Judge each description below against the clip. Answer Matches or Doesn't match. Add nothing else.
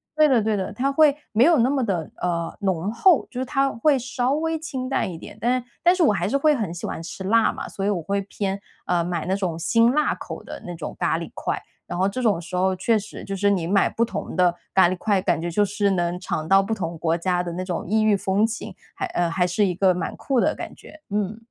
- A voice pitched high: Matches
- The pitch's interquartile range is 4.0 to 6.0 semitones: Matches